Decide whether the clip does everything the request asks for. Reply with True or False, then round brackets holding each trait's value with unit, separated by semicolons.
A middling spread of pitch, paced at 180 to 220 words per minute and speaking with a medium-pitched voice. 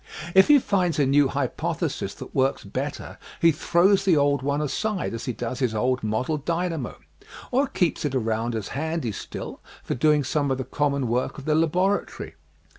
True (4.6 semitones; 185 wpm; 145 Hz)